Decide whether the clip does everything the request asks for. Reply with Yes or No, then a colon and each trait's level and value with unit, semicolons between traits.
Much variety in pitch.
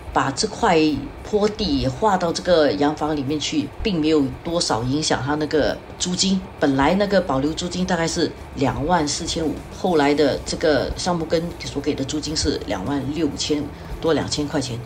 No: average, 3.3 semitones